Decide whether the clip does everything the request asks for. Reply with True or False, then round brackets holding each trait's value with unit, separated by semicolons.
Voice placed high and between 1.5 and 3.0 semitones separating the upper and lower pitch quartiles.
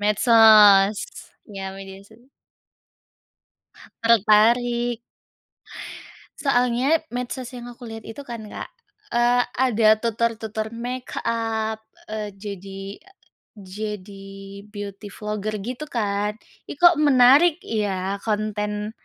True (220 Hz; 2.7 semitones)